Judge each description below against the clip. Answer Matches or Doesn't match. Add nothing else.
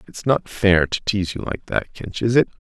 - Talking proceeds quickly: Matches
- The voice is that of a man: Matches